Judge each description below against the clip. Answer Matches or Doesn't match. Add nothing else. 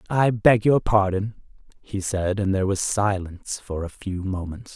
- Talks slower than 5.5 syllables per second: Matches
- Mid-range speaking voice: Doesn't match